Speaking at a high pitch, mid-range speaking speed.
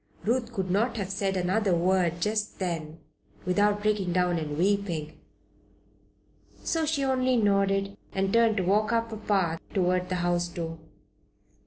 Yes: high, 195 Hz; average, 150 wpm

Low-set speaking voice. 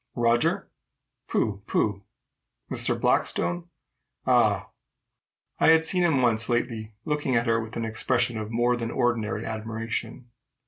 Yes: low, 115 Hz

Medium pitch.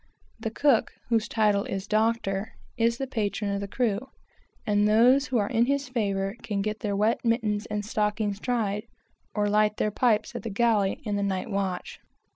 No: high, 215 Hz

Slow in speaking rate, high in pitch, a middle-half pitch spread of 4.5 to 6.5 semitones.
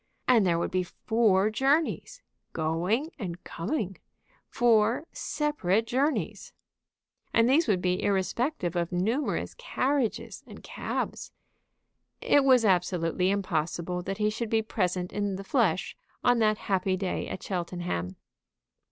Yes: slow, 125 wpm; high, 200 Hz; average, 5.0 semitones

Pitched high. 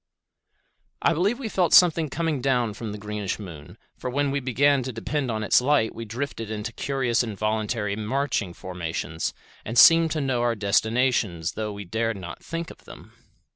No: low, 120 Hz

